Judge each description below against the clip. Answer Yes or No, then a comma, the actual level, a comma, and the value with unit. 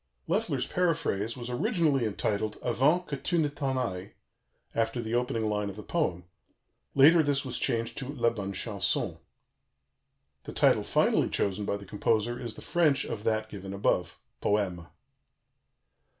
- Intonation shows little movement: No, average, 5.1 semitones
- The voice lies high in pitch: No, low, 115 Hz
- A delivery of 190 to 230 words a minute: No, average, 150 wpm